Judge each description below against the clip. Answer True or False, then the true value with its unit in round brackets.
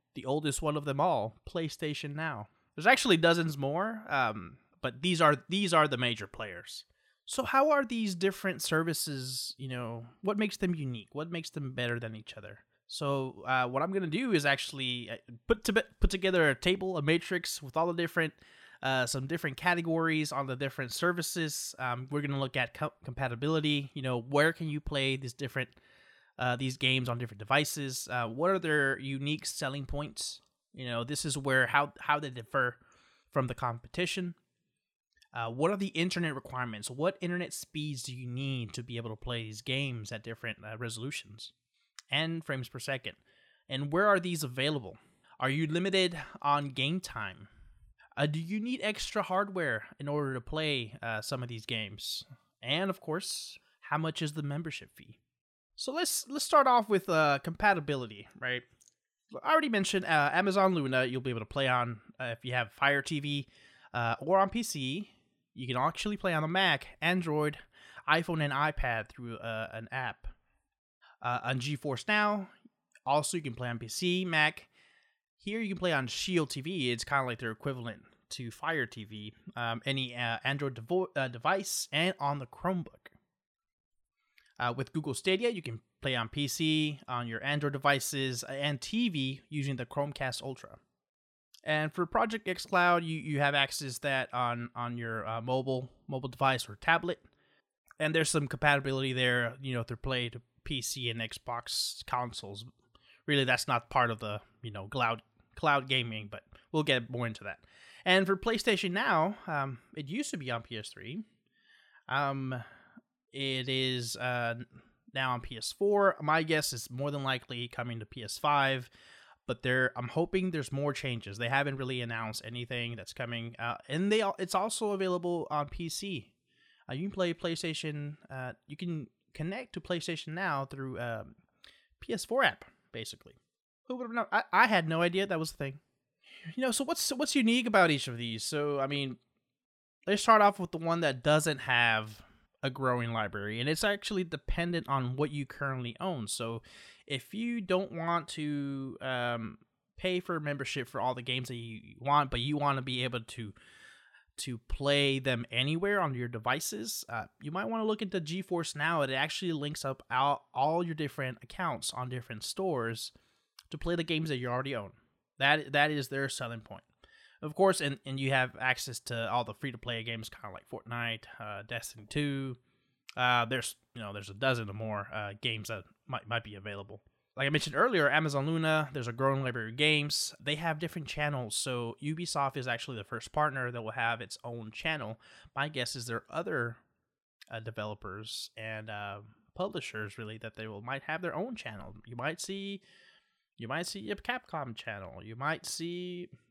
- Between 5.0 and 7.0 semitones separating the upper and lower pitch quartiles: True (5.4 semitones)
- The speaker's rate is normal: True (185 wpm)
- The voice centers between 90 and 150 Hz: True (140 Hz)